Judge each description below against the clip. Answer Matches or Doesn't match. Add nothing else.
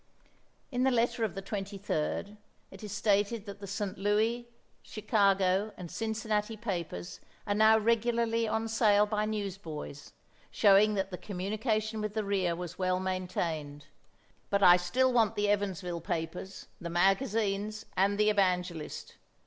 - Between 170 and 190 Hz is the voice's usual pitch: Doesn't match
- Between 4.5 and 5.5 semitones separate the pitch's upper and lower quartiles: Doesn't match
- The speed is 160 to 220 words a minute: Doesn't match